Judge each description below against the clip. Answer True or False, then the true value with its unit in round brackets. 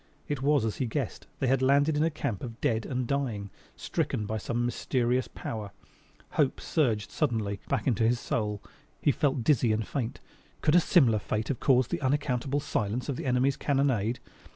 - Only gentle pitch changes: False (3.8 semitones)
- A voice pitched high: False (125 Hz)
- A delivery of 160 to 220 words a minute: True (185 wpm)